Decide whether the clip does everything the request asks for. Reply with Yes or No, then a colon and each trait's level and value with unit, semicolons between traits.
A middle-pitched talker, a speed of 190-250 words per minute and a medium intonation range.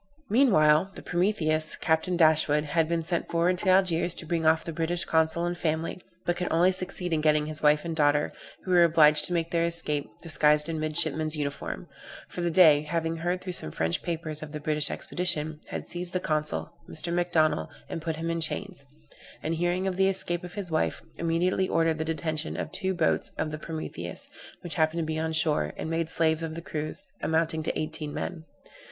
No: medium, 165 Hz; fast, 205 wpm; narrow, 2.0 semitones